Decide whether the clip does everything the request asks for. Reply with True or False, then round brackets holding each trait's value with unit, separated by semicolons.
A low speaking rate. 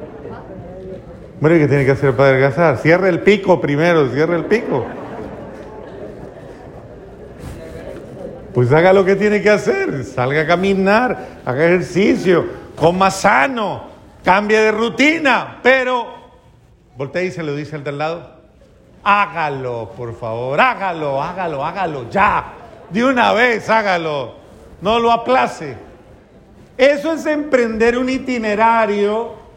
True (120 wpm)